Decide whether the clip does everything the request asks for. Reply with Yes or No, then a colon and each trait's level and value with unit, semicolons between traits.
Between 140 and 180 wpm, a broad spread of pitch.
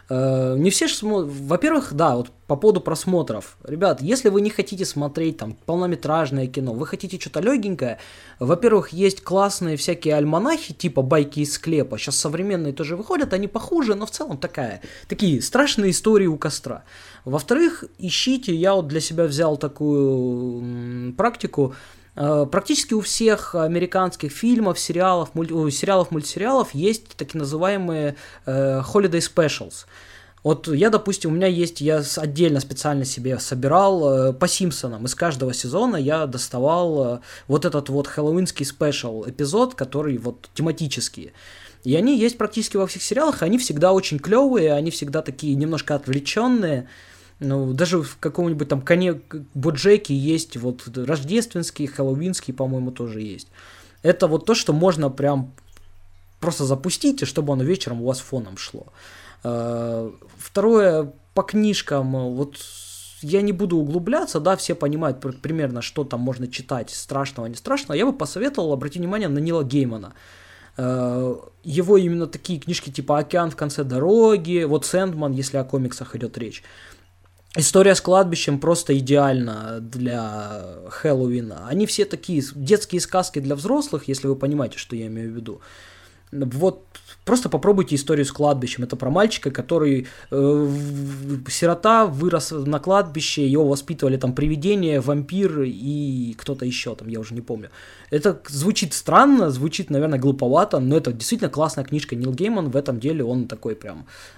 Yes: average, 150 wpm; wide, 5.7 semitones